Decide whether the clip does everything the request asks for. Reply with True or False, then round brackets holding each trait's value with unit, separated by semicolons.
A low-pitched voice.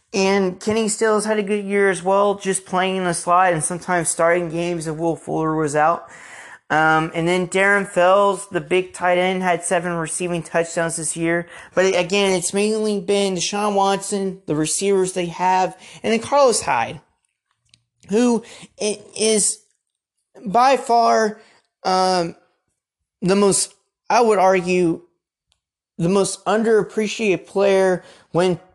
False (185 Hz)